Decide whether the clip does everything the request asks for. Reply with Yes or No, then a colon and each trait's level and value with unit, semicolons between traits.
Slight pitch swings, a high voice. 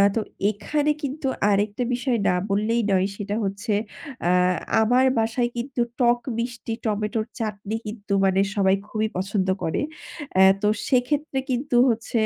No: average, 3.4 semitones; high, 225 Hz